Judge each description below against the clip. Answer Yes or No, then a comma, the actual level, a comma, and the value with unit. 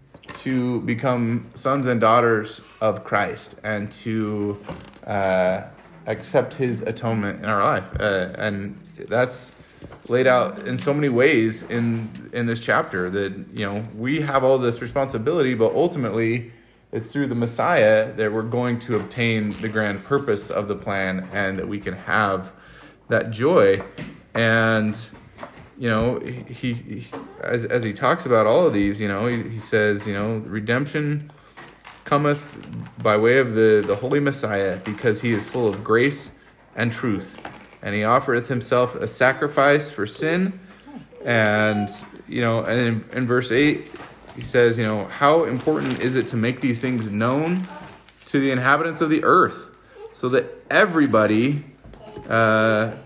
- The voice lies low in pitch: Yes, low, 115 Hz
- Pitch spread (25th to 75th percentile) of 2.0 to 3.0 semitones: No, average, 3.6 semitones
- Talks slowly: No, average, 160 wpm